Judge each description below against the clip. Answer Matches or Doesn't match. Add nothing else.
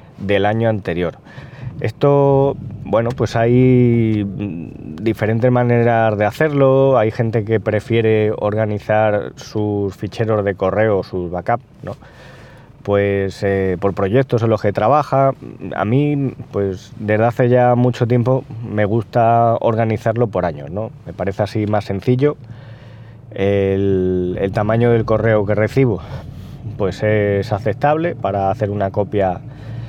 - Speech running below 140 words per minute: Matches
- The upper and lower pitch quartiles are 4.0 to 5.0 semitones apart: Doesn't match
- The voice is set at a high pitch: Doesn't match